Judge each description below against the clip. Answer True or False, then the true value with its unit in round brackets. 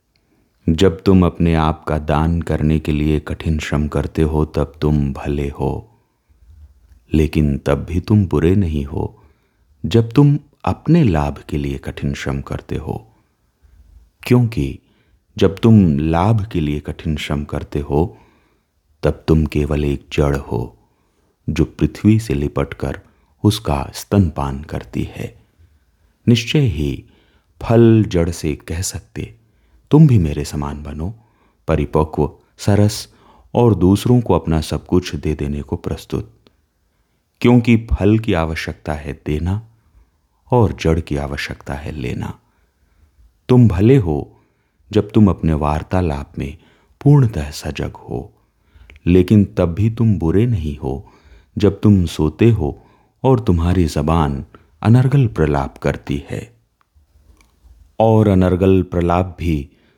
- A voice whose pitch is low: True (80 Hz)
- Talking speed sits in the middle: True (125 wpm)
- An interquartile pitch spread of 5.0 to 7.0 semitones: True (5.6 semitones)